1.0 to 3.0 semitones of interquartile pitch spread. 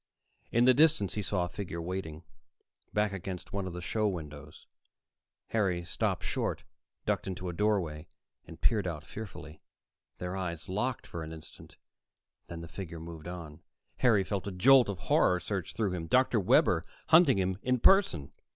No: average, 3.8 semitones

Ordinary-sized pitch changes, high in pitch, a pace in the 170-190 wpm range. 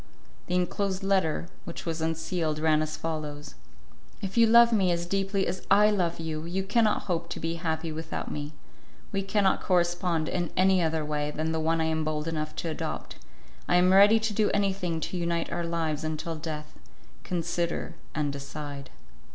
No: average, 3.3 semitones; medium, 170 Hz; average, 180 wpm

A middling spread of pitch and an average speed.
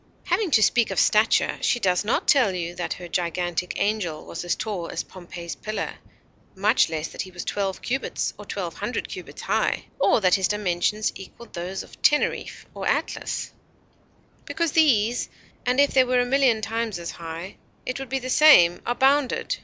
No: wide, 6.0 semitones; average, 185 wpm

